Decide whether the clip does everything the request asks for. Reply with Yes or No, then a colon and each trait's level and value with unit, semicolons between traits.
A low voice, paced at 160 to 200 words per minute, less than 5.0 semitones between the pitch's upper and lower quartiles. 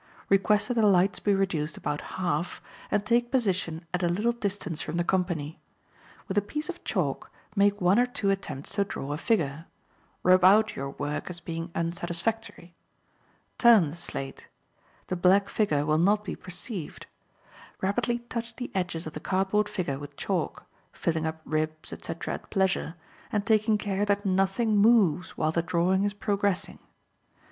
No: high, 190 Hz; average, 170 wpm; average, 3.9 semitones